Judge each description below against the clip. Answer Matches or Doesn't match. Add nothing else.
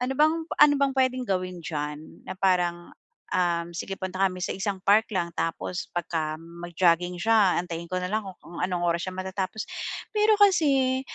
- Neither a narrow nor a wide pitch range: Matches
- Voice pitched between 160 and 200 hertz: Matches